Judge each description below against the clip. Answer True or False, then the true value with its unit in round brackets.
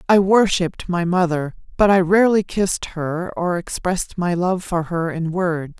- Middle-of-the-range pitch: True (175 Hz)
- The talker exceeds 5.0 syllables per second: False (4.7 syllables/s)